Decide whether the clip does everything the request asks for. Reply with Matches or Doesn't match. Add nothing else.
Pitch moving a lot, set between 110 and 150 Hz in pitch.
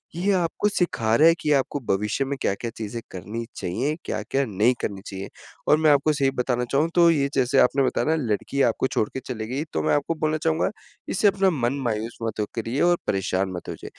Matches